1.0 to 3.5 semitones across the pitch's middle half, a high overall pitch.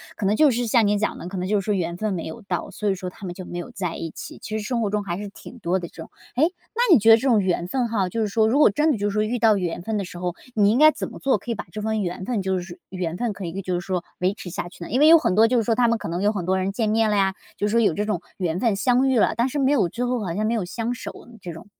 No: average, 4.1 semitones; high, 205 Hz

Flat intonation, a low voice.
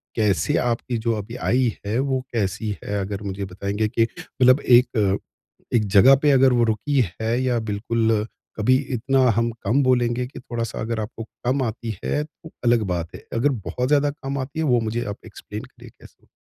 No: average, 3.1 semitones; low, 120 Hz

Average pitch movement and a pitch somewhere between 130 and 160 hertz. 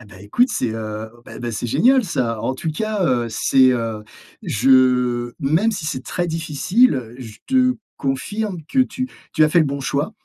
No: wide, 7.7 semitones; low, 135 Hz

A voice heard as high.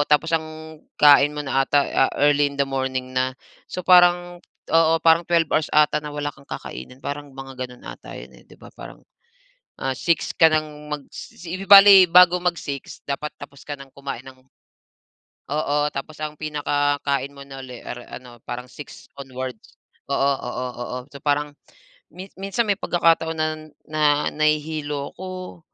No: medium, 150 Hz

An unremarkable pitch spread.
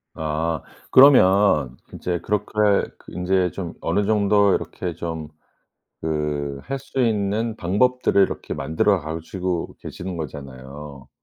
Yes: average, 5.0 semitones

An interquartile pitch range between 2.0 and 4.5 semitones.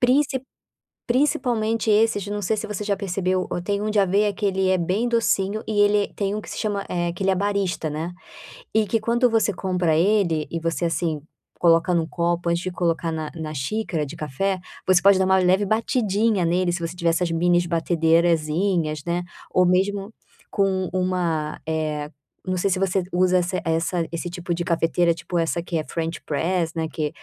Yes: average, 3.3 semitones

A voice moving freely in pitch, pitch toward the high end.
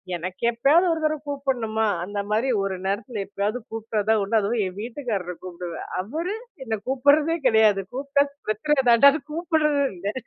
Yes: wide, 5.7 semitones; high, 230 Hz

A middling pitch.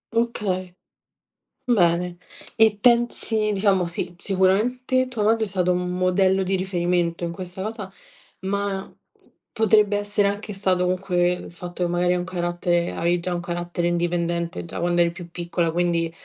Yes: medium, 180 Hz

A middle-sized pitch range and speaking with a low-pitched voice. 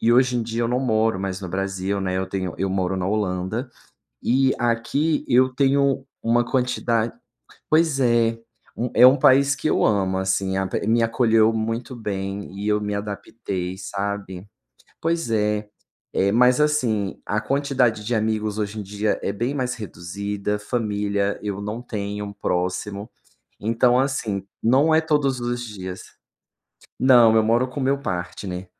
Yes: average, 3.8 semitones; low, 110 Hz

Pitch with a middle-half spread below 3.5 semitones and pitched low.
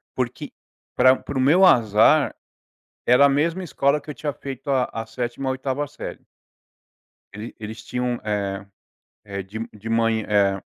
No: average, 4.2 semitones; low, 125 Hz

